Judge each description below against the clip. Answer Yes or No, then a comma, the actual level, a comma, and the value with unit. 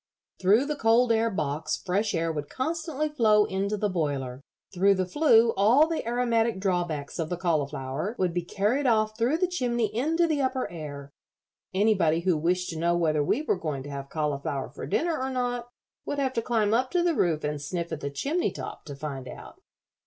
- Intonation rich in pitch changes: Yes, wide, 7.8 semitones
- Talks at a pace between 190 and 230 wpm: Yes, average, 200 wpm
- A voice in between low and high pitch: No, high, 195 Hz